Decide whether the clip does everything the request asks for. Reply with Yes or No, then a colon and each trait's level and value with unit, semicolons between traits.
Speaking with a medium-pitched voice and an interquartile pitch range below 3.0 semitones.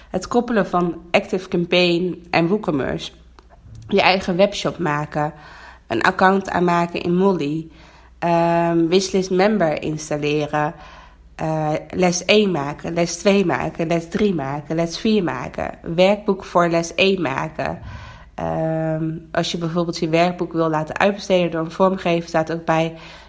Yes: medium, 170 Hz; narrow, 2.6 semitones